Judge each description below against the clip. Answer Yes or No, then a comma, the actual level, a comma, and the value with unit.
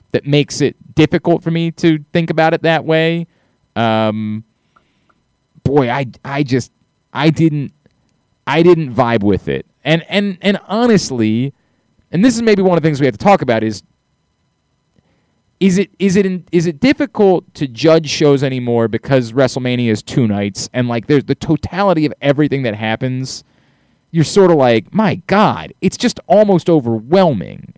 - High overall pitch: No, medium, 150 Hz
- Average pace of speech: Yes, average, 170 wpm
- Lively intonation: Yes, wide, 5.8 semitones